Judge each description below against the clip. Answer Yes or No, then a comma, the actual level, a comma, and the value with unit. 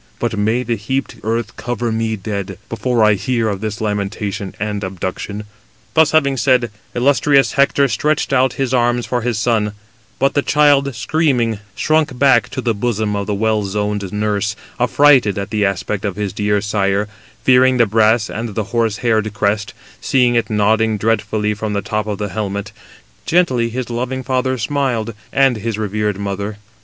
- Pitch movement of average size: Yes, average, 3.3 semitones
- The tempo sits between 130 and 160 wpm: No, average, 170 wpm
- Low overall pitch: Yes, low, 110 Hz